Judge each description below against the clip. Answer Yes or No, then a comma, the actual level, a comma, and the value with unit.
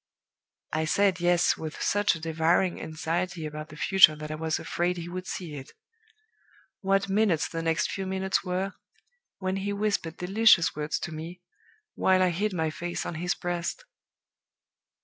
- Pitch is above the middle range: No, medium, 175 Hz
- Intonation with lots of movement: No, average, 3.0 semitones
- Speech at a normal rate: Yes, average, 165 wpm